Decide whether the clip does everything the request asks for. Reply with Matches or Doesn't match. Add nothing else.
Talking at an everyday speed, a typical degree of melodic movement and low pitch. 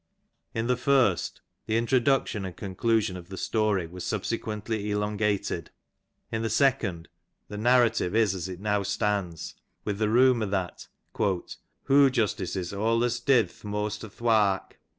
Matches